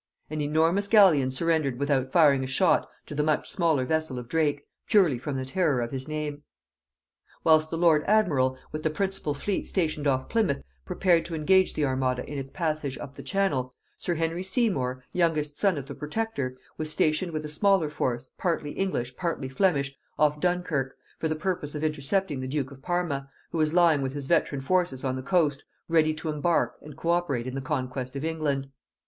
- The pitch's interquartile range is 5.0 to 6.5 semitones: No, average, 3.9 semitones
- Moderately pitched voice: Yes, medium, 150 Hz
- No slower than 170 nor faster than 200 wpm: Yes, average, 195 wpm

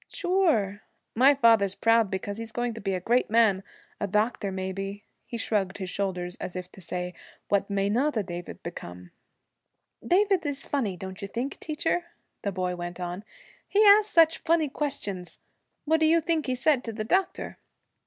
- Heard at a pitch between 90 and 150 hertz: No, high, 215 Hz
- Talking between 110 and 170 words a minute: No, average, 180 wpm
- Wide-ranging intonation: Yes, wide, 7.4 semitones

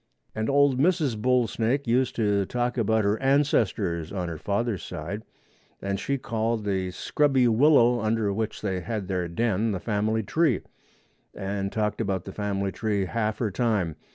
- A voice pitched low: Yes, low, 110 Hz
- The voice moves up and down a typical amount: Yes, average, 3.5 semitones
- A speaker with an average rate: Yes, average, 165 wpm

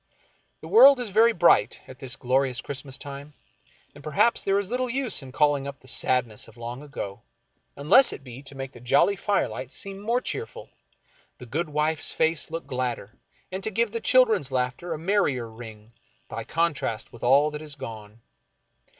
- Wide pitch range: Yes, wide, 7.4 semitones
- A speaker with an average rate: Yes, average, 180 wpm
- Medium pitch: Yes, medium, 145 Hz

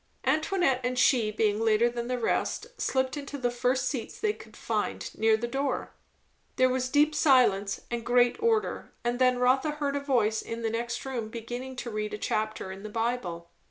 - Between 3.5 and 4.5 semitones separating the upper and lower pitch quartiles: No, average, 2.9 semitones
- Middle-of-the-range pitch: No, high, 245 Hz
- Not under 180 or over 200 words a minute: Yes, average, 195 wpm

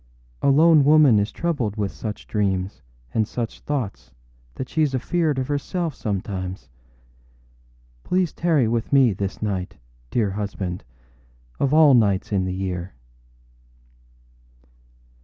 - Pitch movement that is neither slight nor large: No, wide, 6.9 semitones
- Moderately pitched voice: No, low, 110 Hz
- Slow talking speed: Yes, slow, 120 wpm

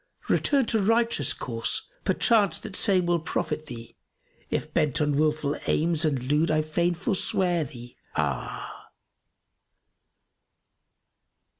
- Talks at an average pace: No, slow, 120 wpm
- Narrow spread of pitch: No, average, 4.1 semitones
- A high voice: No, medium, 160 Hz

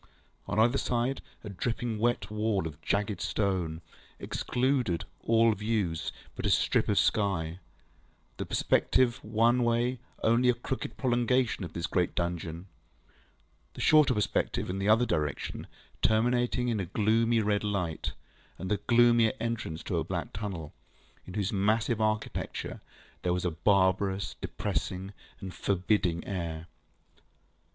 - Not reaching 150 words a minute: Yes, slow, 135 wpm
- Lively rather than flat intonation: No, average, 4.3 semitones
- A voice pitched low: Yes, low, 105 Hz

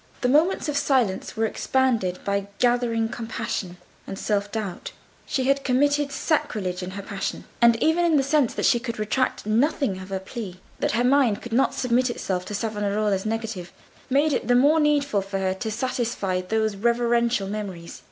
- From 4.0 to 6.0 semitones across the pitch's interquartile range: Yes, average, 4.6 semitones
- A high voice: Yes, high, 225 Hz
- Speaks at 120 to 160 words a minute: No, average, 175 wpm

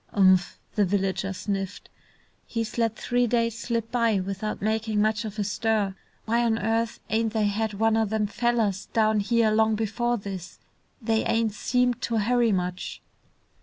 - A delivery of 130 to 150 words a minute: No, average, 165 wpm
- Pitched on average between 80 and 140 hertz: No, high, 220 Hz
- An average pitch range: No, narrow, 2.2 semitones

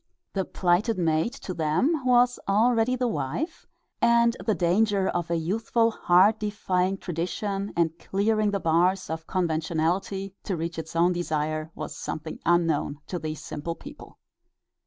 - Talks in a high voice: No, medium, 180 Hz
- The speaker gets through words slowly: No, average, 145 wpm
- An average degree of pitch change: Yes, average, 4.5 semitones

